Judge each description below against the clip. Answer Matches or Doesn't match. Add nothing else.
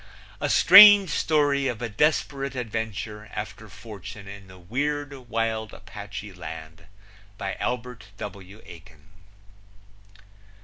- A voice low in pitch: Matches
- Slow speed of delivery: Matches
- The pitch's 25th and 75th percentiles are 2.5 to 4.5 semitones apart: Doesn't match